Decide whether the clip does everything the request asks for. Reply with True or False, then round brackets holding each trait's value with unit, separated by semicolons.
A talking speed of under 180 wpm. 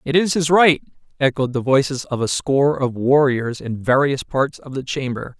False (200 wpm)